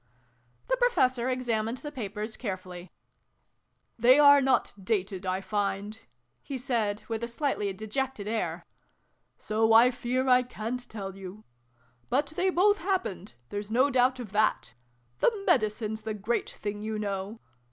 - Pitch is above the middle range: Yes, high, 225 Hz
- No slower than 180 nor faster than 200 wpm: No, average, 150 wpm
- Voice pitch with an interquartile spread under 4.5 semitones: Yes, average, 3.8 semitones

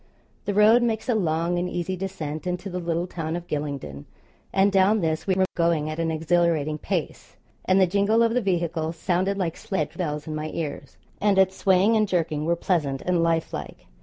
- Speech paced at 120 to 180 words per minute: No, average, 200 wpm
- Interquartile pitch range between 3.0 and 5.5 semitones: Yes, average, 3.4 semitones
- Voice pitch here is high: No, medium, 175 Hz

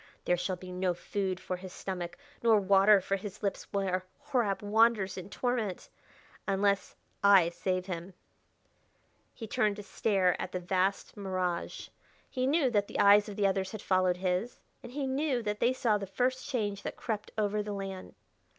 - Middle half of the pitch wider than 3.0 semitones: No, narrow, 2.5 semitones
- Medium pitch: No, high, 200 Hz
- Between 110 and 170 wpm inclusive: No, average, 180 wpm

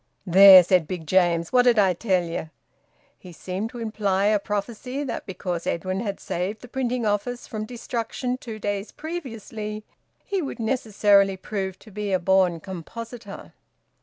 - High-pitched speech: Yes, high, 205 Hz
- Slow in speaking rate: No, average, 160 wpm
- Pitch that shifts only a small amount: No, average, 3.6 semitones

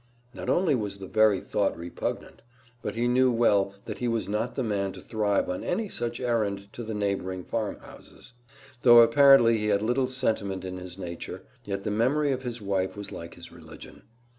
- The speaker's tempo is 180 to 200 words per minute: Yes, average, 190 wpm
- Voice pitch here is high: No, low, 110 Hz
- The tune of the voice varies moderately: Yes, average, 3.5 semitones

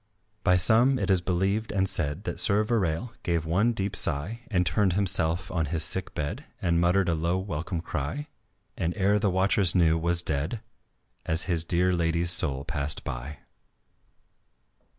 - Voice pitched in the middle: No, very low, 90 Hz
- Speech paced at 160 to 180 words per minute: Yes, average, 165 wpm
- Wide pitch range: No, average, 3.3 semitones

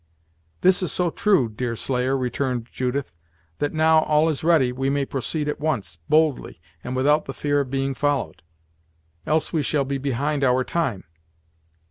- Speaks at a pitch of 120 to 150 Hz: Yes, medium, 140 Hz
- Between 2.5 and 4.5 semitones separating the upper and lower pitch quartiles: Yes, average, 3.2 semitones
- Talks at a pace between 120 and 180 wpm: Yes, average, 160 wpm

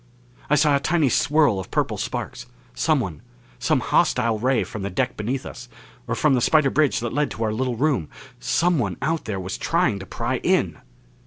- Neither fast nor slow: Yes, average, 190 wpm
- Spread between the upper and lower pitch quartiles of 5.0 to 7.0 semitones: Yes, average, 5.3 semitones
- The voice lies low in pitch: Yes, low, 130 Hz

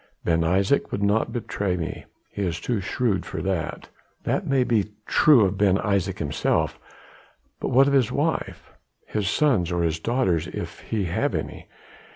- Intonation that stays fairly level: No, average, 4.9 semitones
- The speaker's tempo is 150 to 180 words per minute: Yes, average, 165 wpm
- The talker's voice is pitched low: Yes, low, 100 Hz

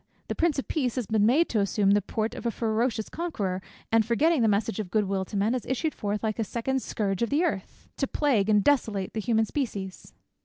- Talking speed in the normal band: No, fast, 235 wpm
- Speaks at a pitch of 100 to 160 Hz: No, high, 220 Hz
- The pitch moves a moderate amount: Yes, average, 4.1 semitones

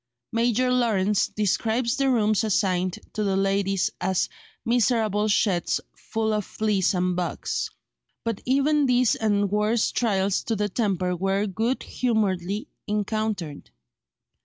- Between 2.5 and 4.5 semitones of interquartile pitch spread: Yes, average, 3.0 semitones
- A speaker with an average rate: No, slow, 125 wpm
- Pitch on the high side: Yes, high, 210 Hz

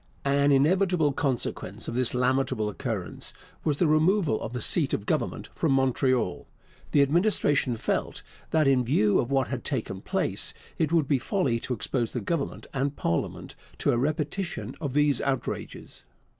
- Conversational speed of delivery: Yes, average, 160 wpm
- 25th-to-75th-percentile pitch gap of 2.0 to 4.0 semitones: Yes, average, 3.6 semitones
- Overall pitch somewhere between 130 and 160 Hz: Yes, low, 135 Hz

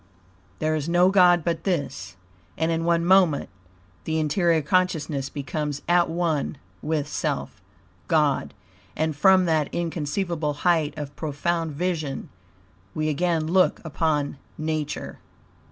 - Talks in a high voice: No, medium, 160 Hz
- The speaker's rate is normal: No, slow, 120 wpm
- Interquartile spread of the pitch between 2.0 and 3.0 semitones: Yes, narrow, 2.6 semitones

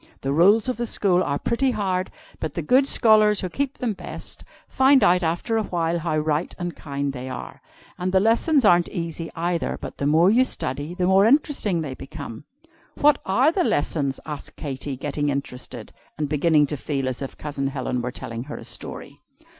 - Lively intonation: Yes, wide, 6.7 semitones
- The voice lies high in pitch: No, medium, 170 Hz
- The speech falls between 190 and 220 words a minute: Yes, average, 195 wpm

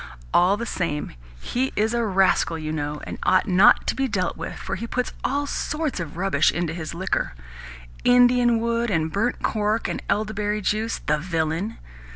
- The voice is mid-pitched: No, high, 200 Hz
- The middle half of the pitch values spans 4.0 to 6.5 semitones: Yes, wide, 5.6 semitones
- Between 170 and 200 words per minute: Yes, average, 180 wpm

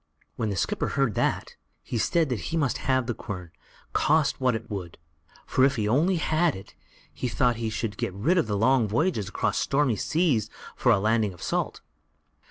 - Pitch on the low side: Yes, low, 120 Hz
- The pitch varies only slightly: No, average, 5.0 semitones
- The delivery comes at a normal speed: Yes, average, 190 wpm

